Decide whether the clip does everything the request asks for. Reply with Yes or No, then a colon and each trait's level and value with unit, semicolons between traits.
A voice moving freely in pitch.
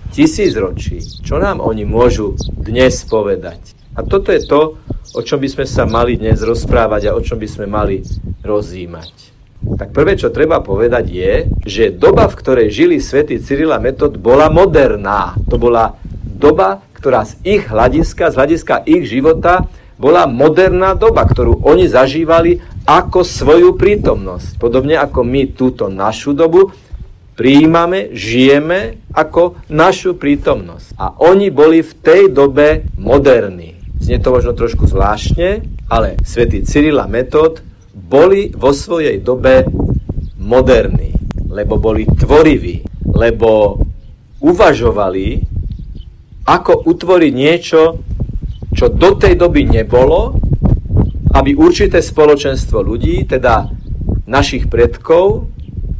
Yes: wide, 8.1 semitones